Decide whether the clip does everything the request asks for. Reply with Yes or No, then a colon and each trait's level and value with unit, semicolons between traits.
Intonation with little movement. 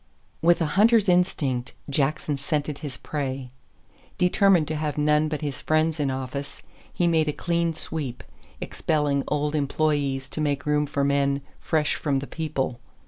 Yes: narrow, 2.1 semitones